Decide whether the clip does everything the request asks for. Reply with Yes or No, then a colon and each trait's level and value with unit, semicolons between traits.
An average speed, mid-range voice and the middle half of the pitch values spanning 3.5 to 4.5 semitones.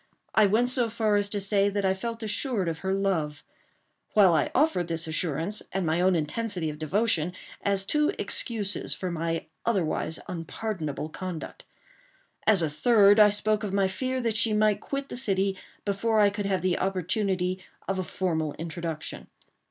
No: average, 175 wpm; high, 195 Hz; average, 4.1 semitones